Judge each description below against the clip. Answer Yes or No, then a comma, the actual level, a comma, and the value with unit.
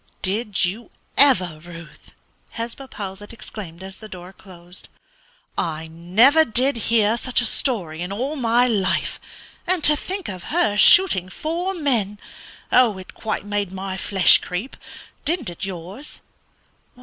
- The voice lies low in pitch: No, high, 205 Hz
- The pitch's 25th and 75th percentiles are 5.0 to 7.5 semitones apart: Yes, wide, 5.6 semitones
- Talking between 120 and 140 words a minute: Yes, slow, 135 wpm